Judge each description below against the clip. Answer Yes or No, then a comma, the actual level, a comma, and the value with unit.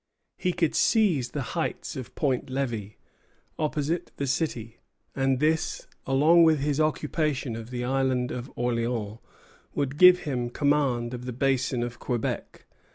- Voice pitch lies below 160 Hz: Yes, low, 135 Hz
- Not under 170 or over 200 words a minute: No, average, 145 wpm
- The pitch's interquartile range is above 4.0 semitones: No, average, 3.6 semitones